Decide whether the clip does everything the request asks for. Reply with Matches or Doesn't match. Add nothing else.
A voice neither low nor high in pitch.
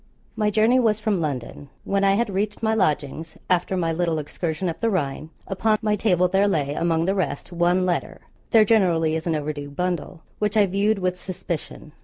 Matches